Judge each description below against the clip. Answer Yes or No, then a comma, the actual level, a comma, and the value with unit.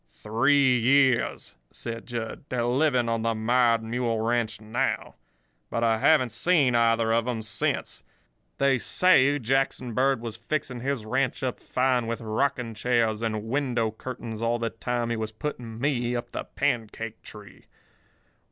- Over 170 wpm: No, average, 150 wpm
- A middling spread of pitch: No, narrow, 2.3 semitones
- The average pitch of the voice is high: No, low, 120 Hz